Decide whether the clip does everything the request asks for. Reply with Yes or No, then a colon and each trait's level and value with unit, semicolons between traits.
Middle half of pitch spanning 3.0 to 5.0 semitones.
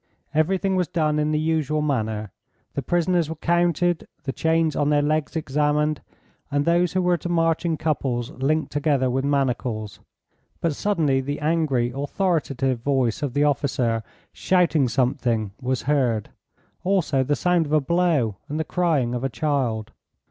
Yes: average, 3.7 semitones